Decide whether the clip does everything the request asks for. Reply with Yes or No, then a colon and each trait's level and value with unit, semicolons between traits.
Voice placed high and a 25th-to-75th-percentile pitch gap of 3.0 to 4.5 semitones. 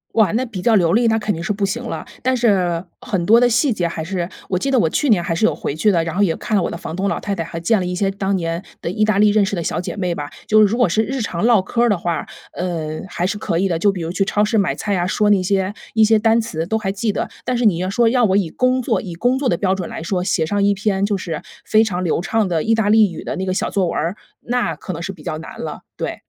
Yes: high, 195 Hz; average, 4.1 semitones